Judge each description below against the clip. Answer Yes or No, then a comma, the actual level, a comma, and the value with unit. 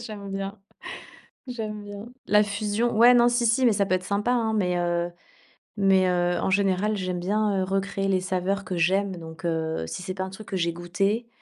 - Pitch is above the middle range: Yes, high, 195 Hz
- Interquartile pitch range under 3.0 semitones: Yes, narrow, 2.6 semitones